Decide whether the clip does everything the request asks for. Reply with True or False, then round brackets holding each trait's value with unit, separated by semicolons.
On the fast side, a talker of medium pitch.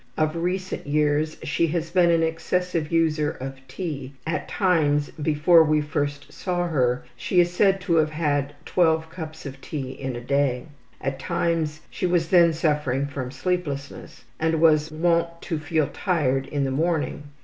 False (165 wpm; 155 Hz)